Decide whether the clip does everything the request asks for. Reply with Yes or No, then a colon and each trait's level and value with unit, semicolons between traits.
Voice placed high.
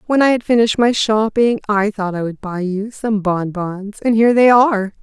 Yes: high, 215 Hz